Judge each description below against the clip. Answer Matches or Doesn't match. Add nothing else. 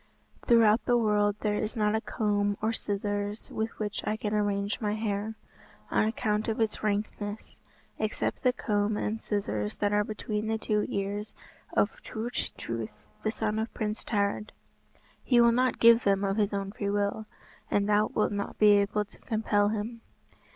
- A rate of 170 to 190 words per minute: Matches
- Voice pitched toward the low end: Doesn't match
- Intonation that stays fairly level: Matches